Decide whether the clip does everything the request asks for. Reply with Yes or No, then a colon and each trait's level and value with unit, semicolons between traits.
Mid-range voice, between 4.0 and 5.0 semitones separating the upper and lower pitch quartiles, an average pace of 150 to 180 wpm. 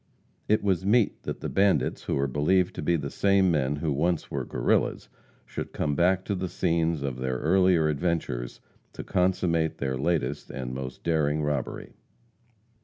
No: very low, 80 Hz; average, 4.7 semitones; average, 170 wpm